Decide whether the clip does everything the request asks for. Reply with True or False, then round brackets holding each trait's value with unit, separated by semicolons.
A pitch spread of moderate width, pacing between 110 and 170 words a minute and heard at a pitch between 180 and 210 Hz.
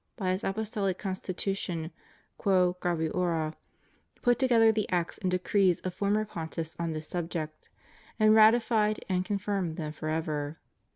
True (4.2 semitones; 135 wpm; 185 Hz)